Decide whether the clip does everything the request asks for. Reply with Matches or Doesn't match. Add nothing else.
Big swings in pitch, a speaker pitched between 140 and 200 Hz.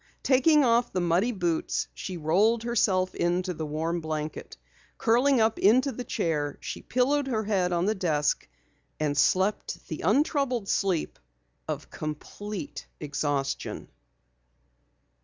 Matches